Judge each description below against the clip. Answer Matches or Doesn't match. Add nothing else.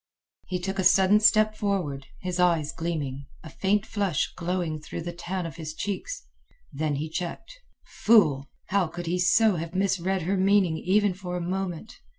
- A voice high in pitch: Doesn't match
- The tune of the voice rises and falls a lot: Doesn't match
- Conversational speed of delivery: Matches